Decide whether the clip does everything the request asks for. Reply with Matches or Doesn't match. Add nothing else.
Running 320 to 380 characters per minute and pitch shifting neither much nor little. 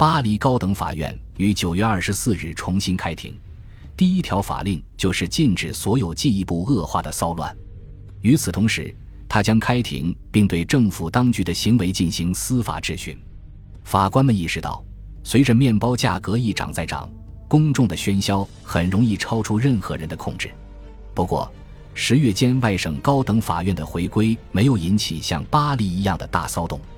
Doesn't match